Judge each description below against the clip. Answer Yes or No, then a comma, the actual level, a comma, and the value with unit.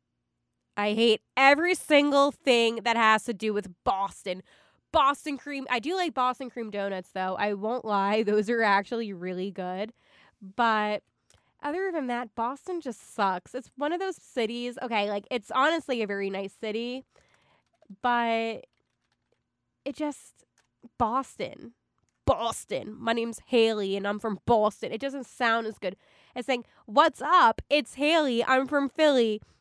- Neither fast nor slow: Yes, average, 150 wpm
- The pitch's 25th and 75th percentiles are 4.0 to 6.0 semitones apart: Yes, average, 4.5 semitones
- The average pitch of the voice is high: Yes, high, 235 Hz